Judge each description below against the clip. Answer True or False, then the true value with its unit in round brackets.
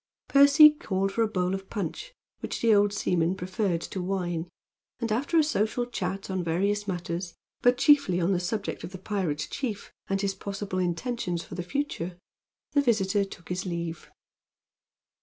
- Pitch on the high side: True (195 Hz)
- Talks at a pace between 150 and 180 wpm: True (170 wpm)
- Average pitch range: True (4.0 semitones)